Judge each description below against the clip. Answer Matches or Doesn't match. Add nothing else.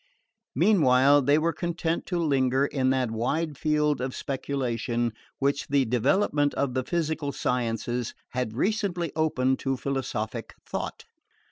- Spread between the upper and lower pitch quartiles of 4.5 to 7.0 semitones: Doesn't match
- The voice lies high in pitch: Doesn't match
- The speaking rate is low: Matches